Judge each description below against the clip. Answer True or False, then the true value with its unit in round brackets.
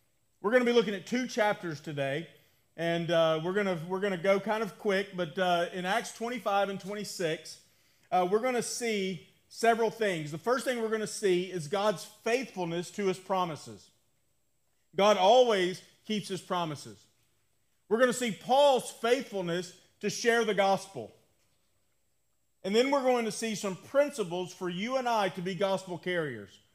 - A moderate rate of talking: True (175 wpm)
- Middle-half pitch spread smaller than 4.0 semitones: False (4.5 semitones)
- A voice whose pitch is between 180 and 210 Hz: True (190 Hz)